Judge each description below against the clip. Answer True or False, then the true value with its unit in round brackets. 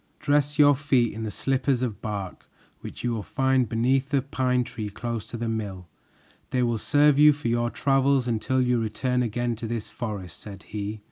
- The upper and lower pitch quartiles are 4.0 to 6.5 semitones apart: False (3.3 semitones)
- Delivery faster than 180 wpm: True (195 wpm)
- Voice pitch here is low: True (120 Hz)